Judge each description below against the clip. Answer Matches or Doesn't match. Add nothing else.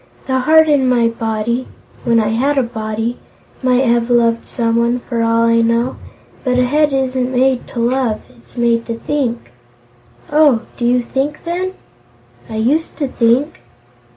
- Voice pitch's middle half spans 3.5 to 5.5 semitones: Doesn't match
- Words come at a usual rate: Matches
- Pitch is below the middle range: Doesn't match